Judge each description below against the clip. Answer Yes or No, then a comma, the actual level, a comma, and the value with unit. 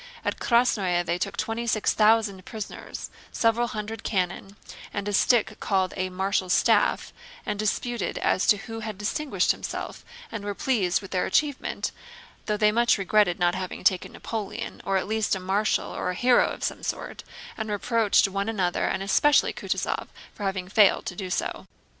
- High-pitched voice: Yes, high, 205 Hz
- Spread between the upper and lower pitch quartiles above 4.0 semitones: No, average, 2.9 semitones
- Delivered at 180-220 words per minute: No, average, 170 wpm